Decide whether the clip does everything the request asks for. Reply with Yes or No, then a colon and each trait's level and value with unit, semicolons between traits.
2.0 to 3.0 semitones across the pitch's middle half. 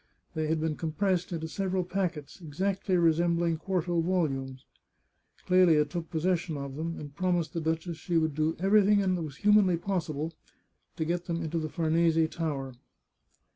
Yes: narrow, 2.4 semitones